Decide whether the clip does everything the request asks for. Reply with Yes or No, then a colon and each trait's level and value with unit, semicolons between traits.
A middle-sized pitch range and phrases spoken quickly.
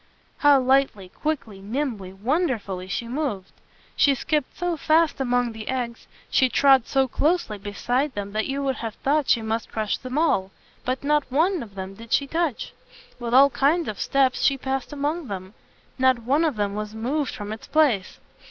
No: average, 5.0 semitones; average, 185 wpm